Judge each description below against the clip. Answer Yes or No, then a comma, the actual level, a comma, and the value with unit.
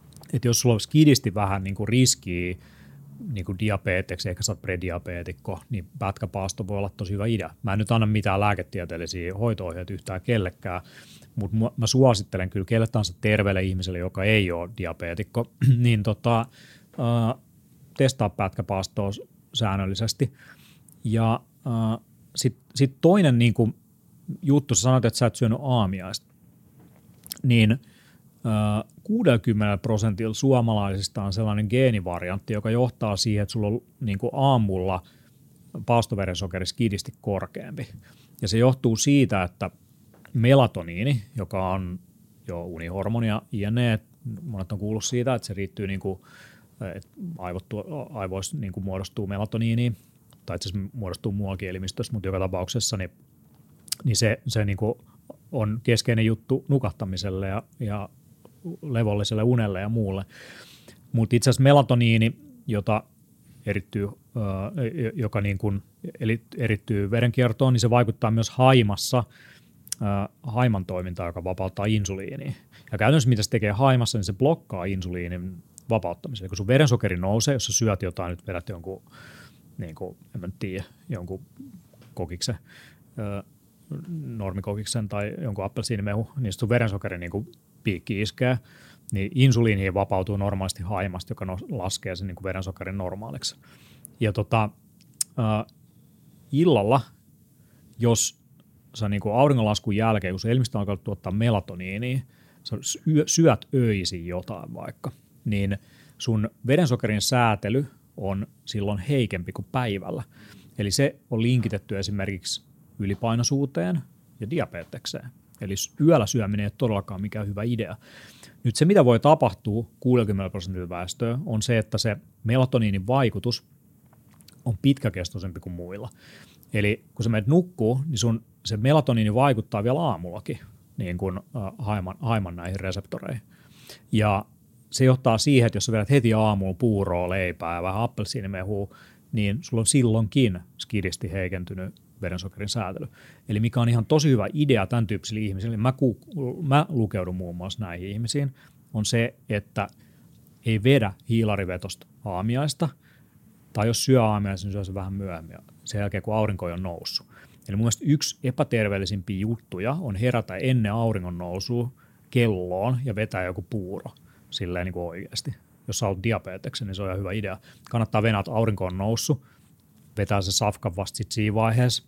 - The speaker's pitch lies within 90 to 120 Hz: Yes, low, 110 Hz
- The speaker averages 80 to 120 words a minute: No, average, 135 wpm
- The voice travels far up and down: No, average, 4.1 semitones